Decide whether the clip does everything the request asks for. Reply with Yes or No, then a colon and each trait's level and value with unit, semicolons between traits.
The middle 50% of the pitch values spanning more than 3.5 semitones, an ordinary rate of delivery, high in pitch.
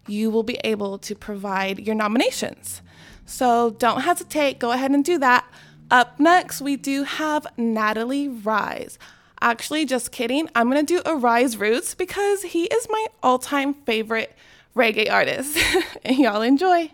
Yes: wide, 5.4 semitones; average, 150 wpm; very high, 255 Hz